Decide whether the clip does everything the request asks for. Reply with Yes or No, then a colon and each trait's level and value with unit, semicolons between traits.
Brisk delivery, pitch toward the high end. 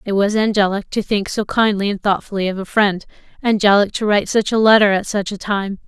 Yes: fast, 215 wpm; high, 205 Hz